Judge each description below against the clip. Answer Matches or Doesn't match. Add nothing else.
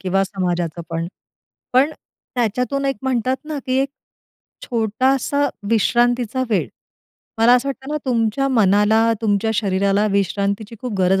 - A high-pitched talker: Matches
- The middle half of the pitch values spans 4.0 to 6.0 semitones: Matches